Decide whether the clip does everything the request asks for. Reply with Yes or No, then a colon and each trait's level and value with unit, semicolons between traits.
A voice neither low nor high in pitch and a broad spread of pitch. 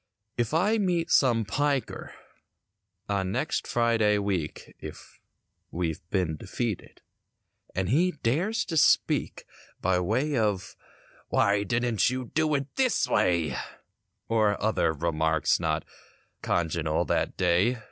No: low, 105 Hz; wide, 7.0 semitones